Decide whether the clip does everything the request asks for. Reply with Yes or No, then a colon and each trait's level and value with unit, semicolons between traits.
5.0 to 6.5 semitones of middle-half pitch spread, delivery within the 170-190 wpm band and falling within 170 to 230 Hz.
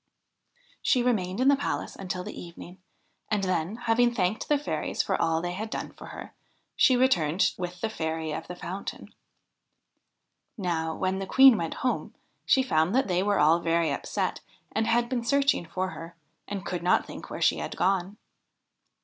Yes: wide, 5.4 semitones; average, 180 wpm; high, 190 Hz